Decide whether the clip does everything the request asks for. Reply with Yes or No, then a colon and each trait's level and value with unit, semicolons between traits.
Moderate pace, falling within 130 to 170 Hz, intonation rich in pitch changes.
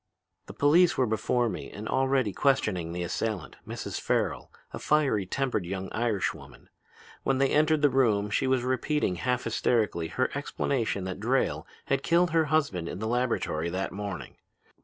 No: average, 165 wpm; low, 120 Hz; wide, 5.7 semitones